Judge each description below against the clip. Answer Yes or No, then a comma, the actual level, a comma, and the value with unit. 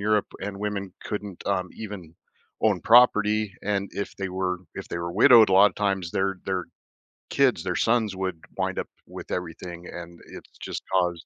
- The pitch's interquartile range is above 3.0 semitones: No, narrow, 2.5 semitones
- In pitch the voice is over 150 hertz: No, very low, 95 Hz